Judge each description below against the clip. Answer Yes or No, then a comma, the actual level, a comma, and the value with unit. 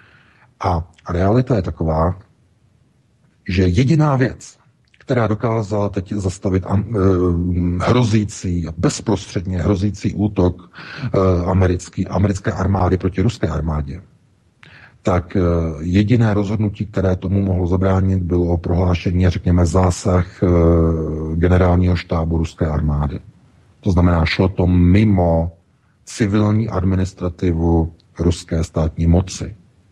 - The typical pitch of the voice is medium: No, very low, 95 Hz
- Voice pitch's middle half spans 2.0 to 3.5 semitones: Yes, average, 2.7 semitones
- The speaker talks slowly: Yes, slow, 105 wpm